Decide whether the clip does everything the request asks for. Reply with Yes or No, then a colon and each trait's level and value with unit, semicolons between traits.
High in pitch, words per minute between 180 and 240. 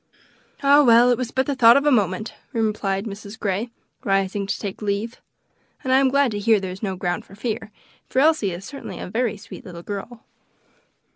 Yes: high, 215 Hz; fast, 205 wpm